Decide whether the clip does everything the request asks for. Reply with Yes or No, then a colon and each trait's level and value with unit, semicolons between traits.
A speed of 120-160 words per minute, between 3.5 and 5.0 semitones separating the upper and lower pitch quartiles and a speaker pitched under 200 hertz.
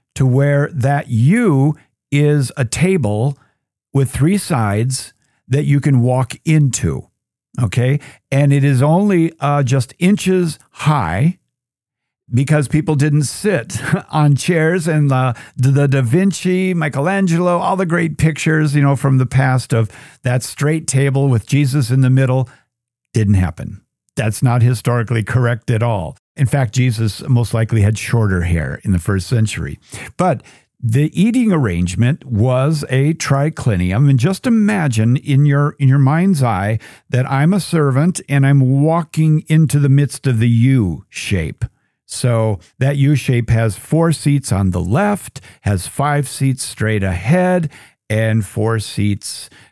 Yes: average, 145 wpm; average, 4.1 semitones; low, 135 Hz